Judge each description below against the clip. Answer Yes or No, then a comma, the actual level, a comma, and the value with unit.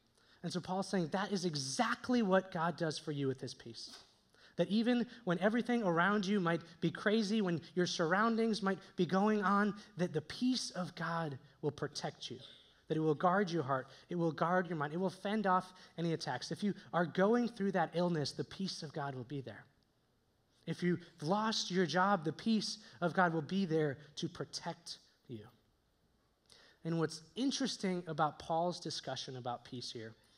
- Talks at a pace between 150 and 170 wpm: No, average, 185 wpm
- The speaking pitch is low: No, medium, 170 Hz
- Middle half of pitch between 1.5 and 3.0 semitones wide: No, average, 4.6 semitones